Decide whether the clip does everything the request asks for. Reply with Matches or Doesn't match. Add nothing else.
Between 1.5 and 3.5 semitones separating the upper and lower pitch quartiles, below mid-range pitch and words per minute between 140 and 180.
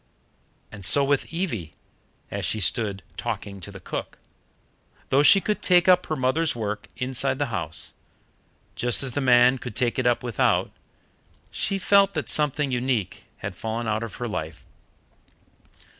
Doesn't match